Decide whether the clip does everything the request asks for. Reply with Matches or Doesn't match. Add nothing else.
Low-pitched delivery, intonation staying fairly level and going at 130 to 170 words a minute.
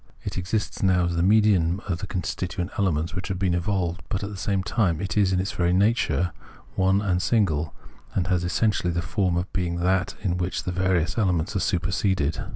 Doesn't match